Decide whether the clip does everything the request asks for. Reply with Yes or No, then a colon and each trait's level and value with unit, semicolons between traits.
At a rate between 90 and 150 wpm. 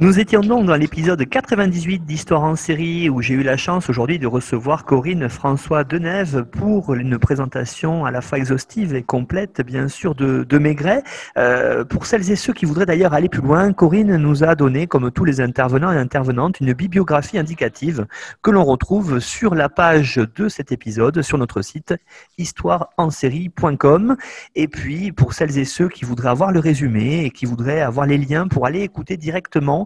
No: average, 185 wpm